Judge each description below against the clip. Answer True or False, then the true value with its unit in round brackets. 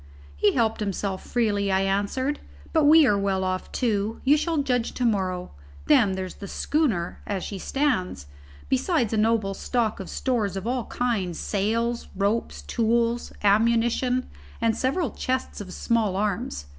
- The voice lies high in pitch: True (220 Hz)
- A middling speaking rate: True (155 wpm)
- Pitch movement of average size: True (4.0 semitones)